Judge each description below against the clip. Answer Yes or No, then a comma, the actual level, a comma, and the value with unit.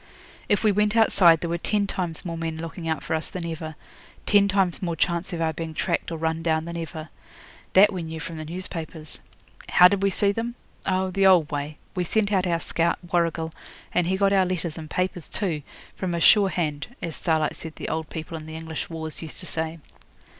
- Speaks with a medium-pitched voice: Yes, medium, 170 Hz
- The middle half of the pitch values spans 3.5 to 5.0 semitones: No, average, 2.7 semitones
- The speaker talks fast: Yes, fast, 220 wpm